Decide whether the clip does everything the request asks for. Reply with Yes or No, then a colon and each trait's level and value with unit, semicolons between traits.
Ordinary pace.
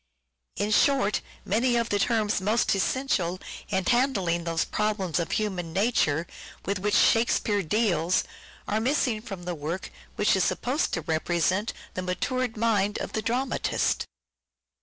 Yes: average, 150 wpm